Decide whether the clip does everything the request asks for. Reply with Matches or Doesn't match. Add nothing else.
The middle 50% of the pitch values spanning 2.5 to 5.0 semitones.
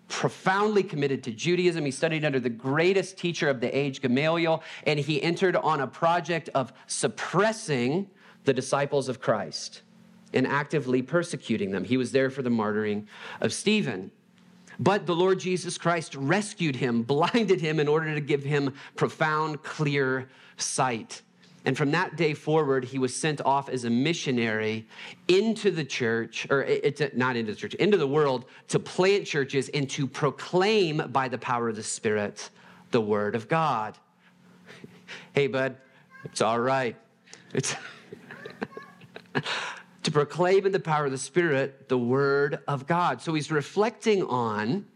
Doesn't match